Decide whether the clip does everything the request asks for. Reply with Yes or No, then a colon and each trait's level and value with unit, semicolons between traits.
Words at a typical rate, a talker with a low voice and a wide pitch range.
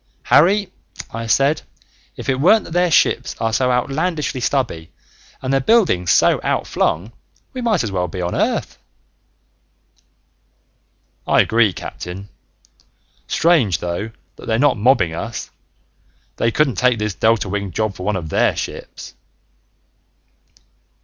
No: slow, 130 wpm; low, 115 Hz; wide, 6.9 semitones